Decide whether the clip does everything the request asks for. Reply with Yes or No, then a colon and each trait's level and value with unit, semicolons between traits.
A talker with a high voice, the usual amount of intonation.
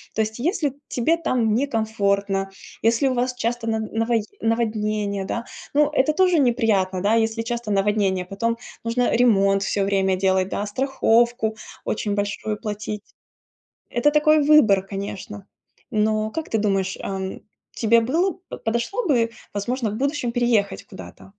Yes: high, 225 Hz; average, 3.3 semitones